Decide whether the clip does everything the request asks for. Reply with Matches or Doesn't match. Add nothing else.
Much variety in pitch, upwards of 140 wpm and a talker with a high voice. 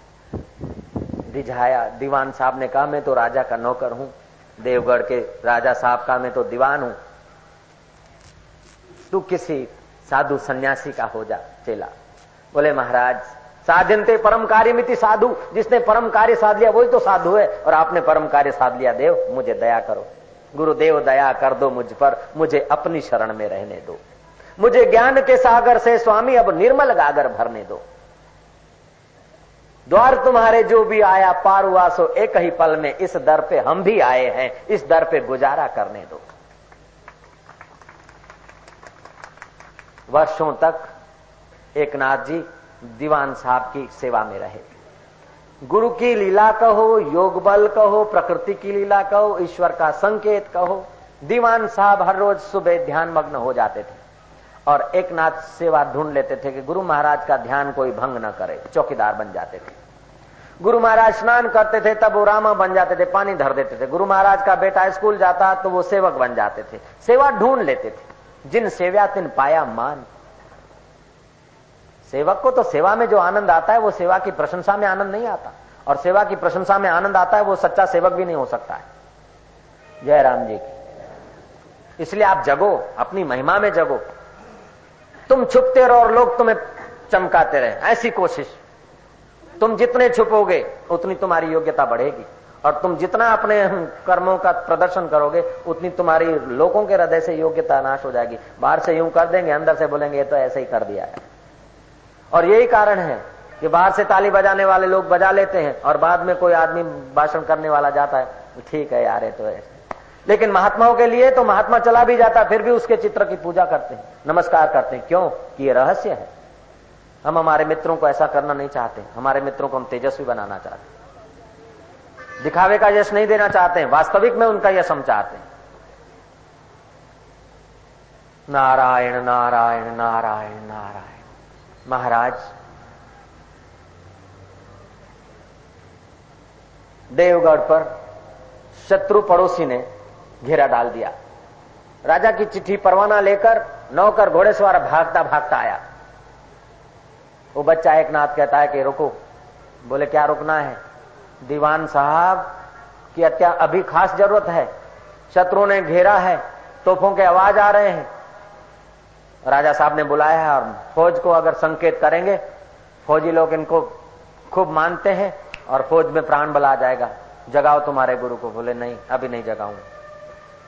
Doesn't match